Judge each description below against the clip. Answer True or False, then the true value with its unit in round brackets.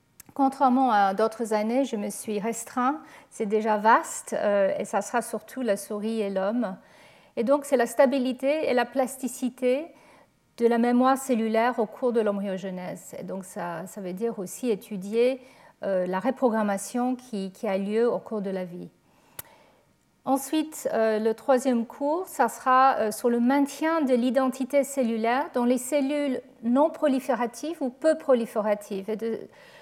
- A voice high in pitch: True (245 Hz)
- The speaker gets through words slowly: False (155 wpm)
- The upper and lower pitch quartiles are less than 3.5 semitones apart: False (3.8 semitones)